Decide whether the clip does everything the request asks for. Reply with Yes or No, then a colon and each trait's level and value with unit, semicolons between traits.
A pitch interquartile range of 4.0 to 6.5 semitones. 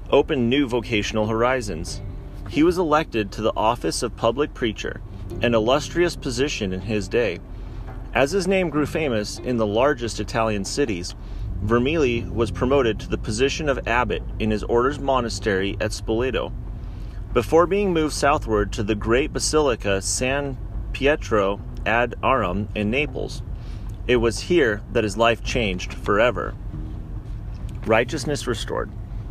Yes: average, 4.3 semitones